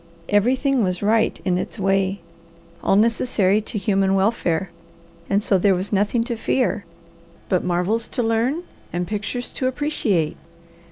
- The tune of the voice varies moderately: Yes, average, 3.4 semitones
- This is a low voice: No, high, 205 Hz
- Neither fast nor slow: Yes, average, 145 wpm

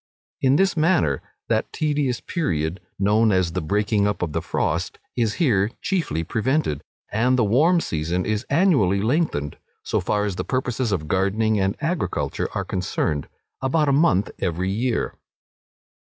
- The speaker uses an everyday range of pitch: No, wide, 7.0 semitones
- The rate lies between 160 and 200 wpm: No, average, 150 wpm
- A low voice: Yes, low, 110 Hz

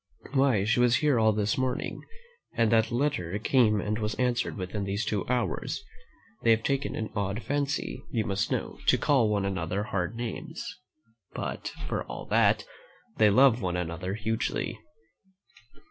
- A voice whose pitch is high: No, low, 110 Hz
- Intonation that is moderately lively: Yes, average, 3.4 semitones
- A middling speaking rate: Yes, average, 160 wpm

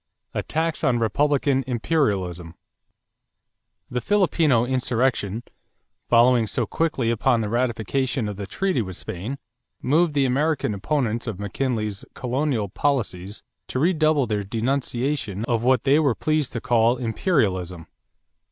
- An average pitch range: Yes, average, 4.7 semitones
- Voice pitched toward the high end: No, low, 125 Hz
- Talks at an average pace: No, slow, 125 wpm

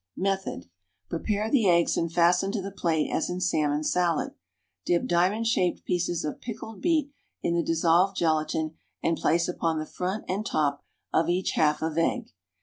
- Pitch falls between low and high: Yes, medium, 175 Hz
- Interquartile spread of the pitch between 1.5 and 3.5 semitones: Yes, average, 3.2 semitones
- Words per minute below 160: No, average, 170 wpm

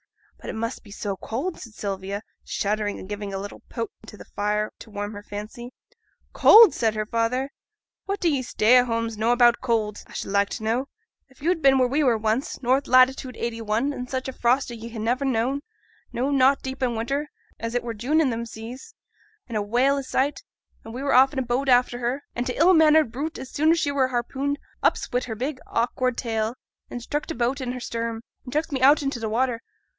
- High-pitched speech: Yes, high, 245 Hz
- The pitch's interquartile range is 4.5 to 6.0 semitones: No, average, 3.3 semitones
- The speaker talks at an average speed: No, fast, 230 wpm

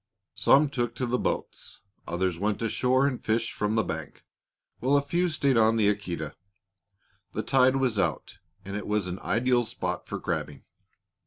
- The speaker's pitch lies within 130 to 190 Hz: No, low, 115 Hz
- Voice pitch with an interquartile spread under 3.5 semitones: No, average, 4.4 semitones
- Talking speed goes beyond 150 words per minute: Yes, average, 170 wpm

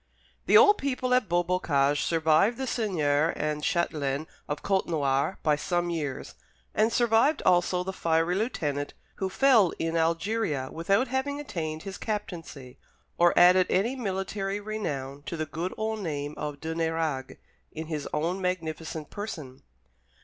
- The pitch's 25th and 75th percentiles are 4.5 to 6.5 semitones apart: Yes, average, 5.1 semitones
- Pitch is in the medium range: Yes, medium, 170 Hz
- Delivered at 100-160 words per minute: Yes, average, 140 wpm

